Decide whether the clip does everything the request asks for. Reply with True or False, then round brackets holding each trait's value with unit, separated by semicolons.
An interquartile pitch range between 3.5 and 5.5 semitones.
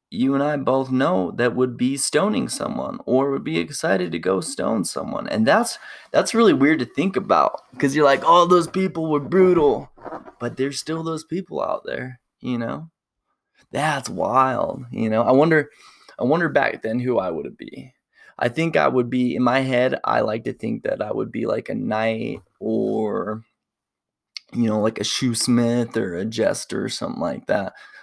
True (4.5 semitones)